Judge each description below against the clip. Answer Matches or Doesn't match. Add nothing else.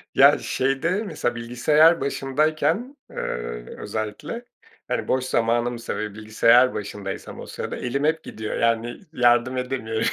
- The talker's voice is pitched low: Matches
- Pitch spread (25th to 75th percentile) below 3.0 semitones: Doesn't match